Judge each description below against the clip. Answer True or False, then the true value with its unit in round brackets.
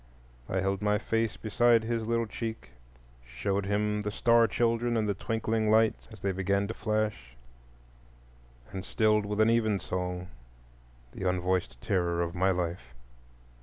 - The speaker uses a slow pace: False (150 wpm)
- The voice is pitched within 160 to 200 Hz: False (105 Hz)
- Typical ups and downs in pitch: True (3.3 semitones)